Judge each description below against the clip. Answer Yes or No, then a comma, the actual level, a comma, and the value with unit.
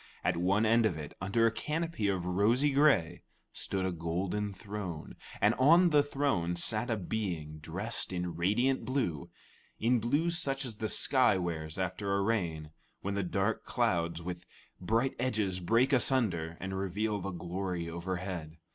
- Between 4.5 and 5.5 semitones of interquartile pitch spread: Yes, average, 5.0 semitones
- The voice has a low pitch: Yes, low, 100 Hz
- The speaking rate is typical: Yes, average, 160 wpm